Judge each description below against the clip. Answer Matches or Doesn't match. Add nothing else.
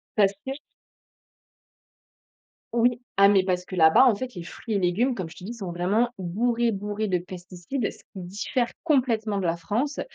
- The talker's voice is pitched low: Doesn't match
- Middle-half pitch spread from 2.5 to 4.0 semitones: Doesn't match